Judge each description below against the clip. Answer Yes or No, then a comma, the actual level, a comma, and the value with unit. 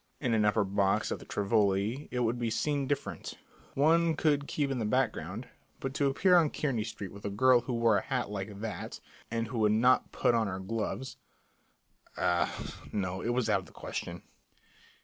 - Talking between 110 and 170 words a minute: No, average, 195 wpm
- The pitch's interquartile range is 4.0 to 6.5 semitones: Yes, average, 4.5 semitones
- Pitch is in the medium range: No, low, 115 Hz